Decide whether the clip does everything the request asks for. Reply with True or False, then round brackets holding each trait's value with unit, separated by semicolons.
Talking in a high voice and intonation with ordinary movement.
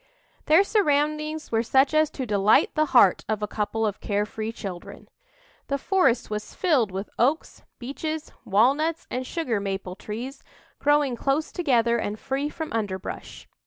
False (250 Hz; 6.3 semitones)